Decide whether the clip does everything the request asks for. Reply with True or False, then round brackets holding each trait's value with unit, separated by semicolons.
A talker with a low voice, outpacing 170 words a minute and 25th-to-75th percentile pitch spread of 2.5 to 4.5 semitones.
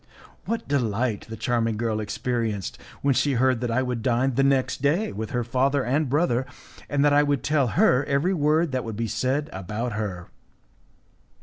True (125 Hz; 185 wpm; 3.8 semitones)